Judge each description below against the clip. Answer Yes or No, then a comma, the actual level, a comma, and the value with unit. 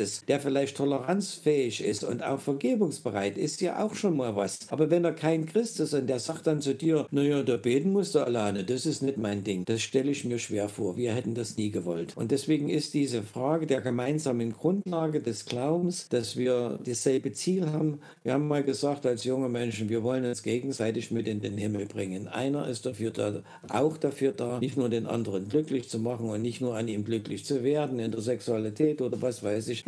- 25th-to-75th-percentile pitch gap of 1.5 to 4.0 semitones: No, average, 4.5 semitones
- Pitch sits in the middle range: No, low, 130 Hz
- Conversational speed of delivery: No, fast, 215 wpm